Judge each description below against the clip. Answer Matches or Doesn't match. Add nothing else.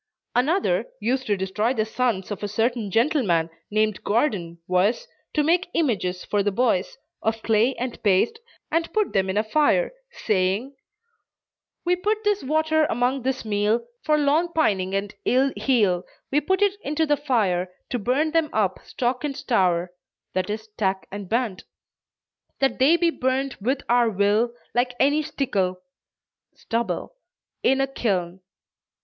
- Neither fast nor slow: Matches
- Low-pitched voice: Doesn't match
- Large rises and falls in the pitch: Matches